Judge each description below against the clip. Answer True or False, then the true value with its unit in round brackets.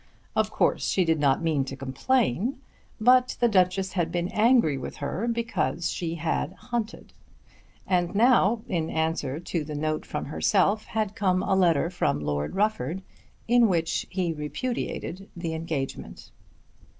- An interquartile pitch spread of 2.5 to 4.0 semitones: False (5.4 semitones)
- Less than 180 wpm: True (150 wpm)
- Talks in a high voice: False (175 Hz)